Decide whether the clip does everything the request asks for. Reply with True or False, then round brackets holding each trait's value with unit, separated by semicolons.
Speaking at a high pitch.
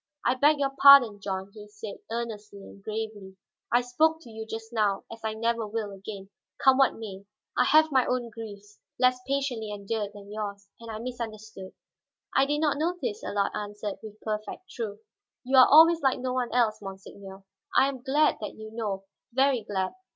True (220 Hz)